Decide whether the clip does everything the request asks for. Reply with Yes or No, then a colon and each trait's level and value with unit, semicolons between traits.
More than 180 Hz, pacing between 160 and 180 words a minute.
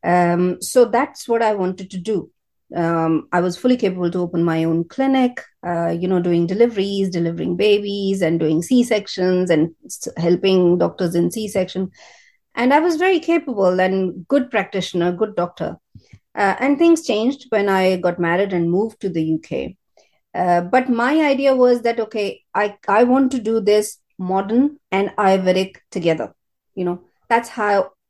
Yes: high, 190 Hz; average, 165 wpm